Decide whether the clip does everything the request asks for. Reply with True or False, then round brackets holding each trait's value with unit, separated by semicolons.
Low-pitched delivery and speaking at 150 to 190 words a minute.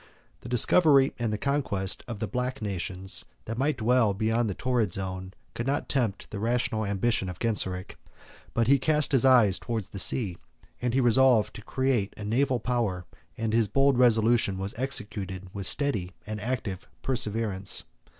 True (115 Hz; 160 wpm)